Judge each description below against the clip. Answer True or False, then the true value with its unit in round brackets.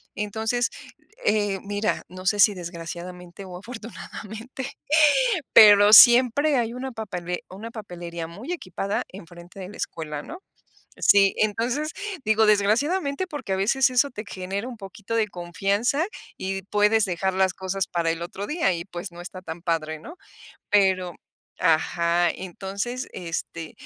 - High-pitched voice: True (195 Hz)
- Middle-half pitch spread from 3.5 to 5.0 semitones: True (4.0 semitones)